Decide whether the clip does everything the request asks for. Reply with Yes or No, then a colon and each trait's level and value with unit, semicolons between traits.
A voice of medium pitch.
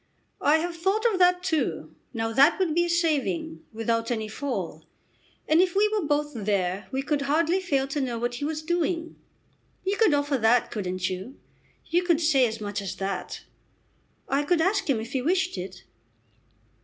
No: very high, 290 Hz